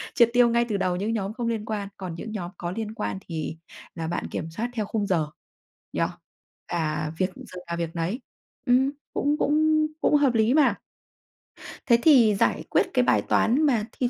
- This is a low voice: No, high, 215 Hz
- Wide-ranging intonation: Yes, wide, 5.9 semitones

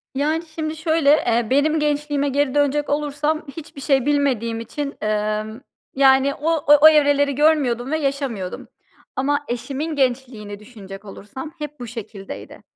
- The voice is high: Yes, very high, 280 Hz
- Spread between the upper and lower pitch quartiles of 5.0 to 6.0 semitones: No, average, 3.8 semitones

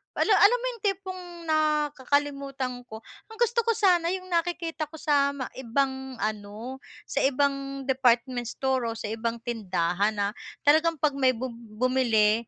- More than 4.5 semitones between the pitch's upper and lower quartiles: Yes, average, 5.1 semitones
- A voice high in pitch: Yes, very high, 270 Hz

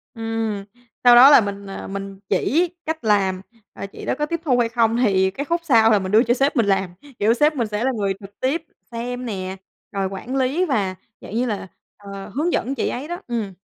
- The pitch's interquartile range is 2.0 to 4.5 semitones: No, average, 5.0 semitones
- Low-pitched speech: No, high, 225 Hz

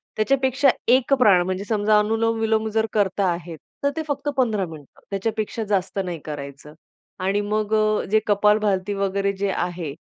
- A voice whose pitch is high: Yes, high, 205 Hz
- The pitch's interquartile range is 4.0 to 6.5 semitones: No, average, 2.9 semitones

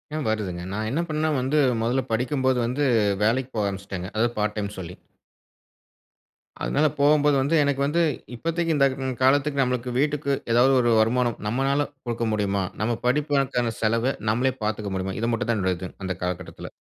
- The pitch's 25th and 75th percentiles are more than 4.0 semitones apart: Yes, average, 4.5 semitones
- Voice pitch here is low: Yes, low, 120 Hz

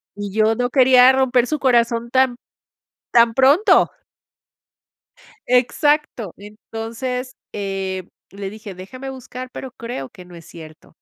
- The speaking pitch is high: Yes, high, 235 Hz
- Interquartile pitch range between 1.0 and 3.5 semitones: No, average, 4.2 semitones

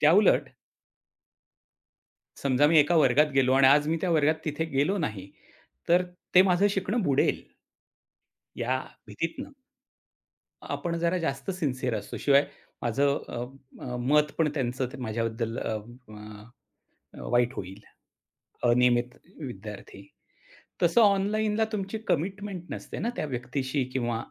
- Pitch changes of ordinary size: No, wide, 6.2 semitones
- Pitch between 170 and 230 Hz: No, medium, 140 Hz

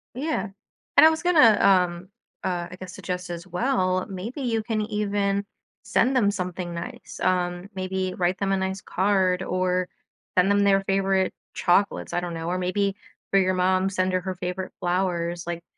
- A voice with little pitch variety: Yes, narrow, 1.7 semitones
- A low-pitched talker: No, medium, 185 Hz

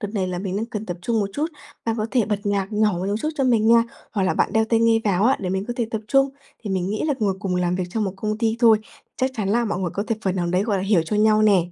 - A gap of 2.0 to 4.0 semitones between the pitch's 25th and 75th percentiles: Yes, average, 3.0 semitones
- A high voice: Yes, high, 210 Hz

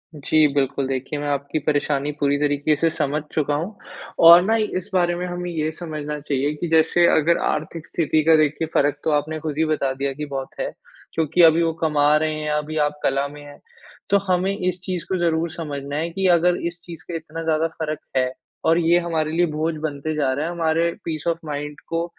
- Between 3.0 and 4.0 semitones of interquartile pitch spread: No, narrow, 2.4 semitones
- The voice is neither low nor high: Yes, medium, 155 Hz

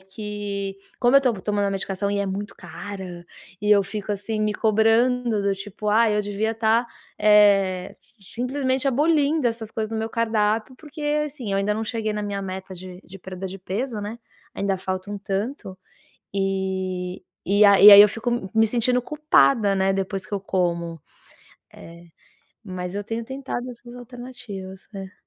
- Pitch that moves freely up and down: No, average, 3.2 semitones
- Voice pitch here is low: No, high, 210 Hz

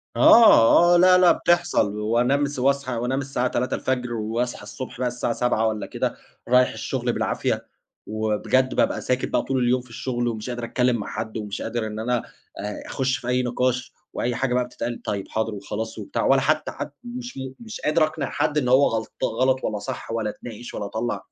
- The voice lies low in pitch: Yes, low, 125 Hz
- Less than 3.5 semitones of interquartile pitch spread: Yes, average, 2.9 semitones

